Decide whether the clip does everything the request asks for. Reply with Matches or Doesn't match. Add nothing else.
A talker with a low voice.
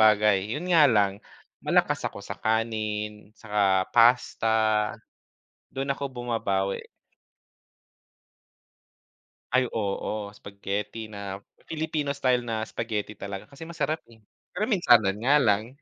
Matches